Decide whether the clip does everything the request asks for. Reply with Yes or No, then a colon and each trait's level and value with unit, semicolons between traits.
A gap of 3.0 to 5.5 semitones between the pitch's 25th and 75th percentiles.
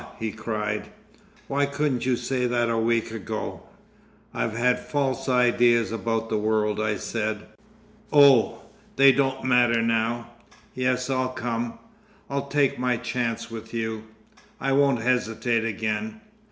No: narrow, 2.4 semitones